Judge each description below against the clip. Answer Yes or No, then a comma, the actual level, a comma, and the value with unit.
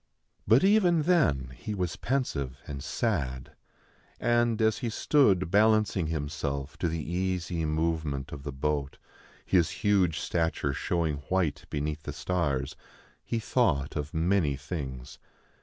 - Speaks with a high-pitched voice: No, very low, 80 Hz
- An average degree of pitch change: No, wide, 6.3 semitones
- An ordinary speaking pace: No, slow, 130 wpm